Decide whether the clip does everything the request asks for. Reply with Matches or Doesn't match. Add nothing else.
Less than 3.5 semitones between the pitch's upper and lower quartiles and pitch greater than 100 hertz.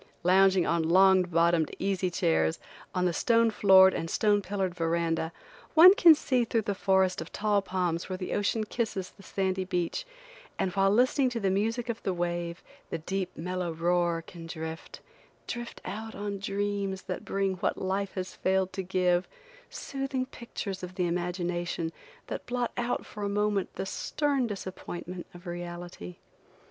Matches